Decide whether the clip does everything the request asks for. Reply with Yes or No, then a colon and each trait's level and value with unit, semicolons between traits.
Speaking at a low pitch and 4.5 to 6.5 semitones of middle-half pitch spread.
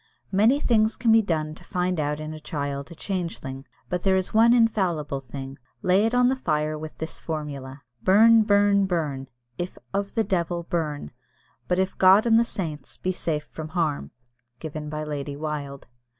No: medium, 170 Hz; average, 5.0 semitones